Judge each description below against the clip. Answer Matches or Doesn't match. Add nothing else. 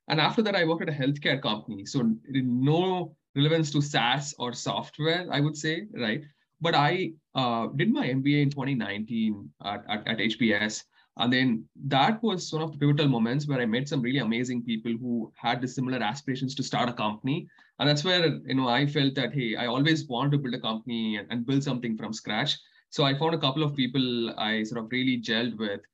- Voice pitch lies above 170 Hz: Doesn't match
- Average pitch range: Matches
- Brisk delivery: Matches